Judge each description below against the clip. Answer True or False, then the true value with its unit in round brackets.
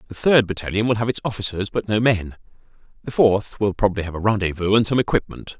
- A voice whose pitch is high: False (105 Hz)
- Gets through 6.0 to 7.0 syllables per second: True (6.4 syllables/s)